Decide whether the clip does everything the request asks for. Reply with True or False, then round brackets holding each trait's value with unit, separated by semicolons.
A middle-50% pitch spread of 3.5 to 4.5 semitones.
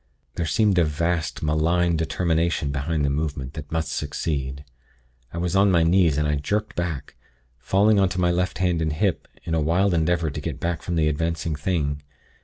False (2.7 semitones)